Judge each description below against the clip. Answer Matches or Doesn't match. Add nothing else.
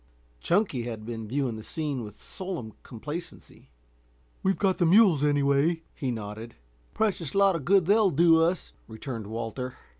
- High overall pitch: Doesn't match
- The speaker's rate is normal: Matches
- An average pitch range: Doesn't match